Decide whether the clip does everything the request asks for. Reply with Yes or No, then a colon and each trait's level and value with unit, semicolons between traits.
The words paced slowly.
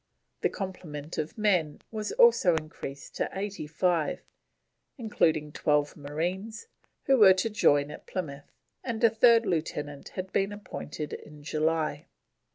Yes: slow, 130 wpm